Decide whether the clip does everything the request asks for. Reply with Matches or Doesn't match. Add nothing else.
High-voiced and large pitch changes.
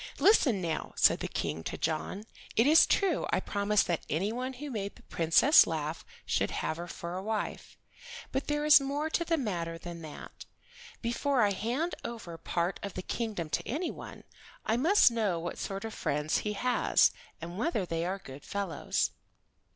Matches